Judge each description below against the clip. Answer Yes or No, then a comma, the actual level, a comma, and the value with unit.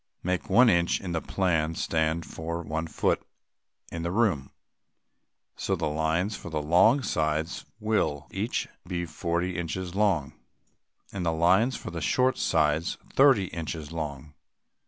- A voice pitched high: No, very low, 85 Hz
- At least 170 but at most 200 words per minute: No, average, 145 wpm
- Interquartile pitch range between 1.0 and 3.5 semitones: Yes, average, 2.8 semitones